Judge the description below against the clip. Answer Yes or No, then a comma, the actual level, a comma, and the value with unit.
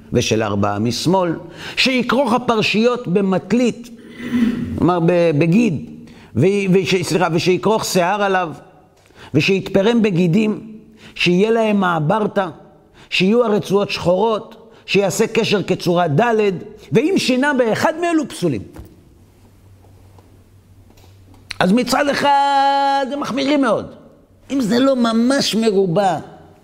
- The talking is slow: Yes, slow, 95 wpm